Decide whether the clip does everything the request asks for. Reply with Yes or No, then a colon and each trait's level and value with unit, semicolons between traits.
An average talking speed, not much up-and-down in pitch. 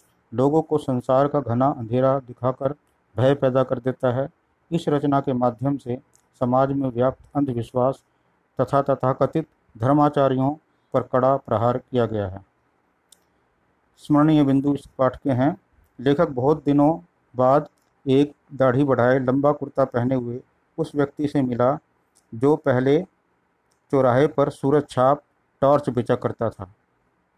Yes: average, 135 wpm; narrow, 2.3 semitones